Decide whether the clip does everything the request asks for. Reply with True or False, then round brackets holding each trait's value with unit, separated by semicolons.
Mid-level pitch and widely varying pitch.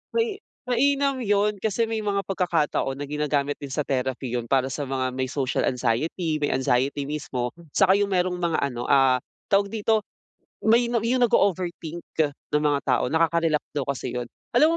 True (160 Hz; 7.2 semitones)